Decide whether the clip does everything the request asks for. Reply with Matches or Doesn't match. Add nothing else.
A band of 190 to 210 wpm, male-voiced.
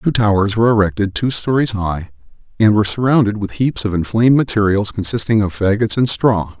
Doesn't match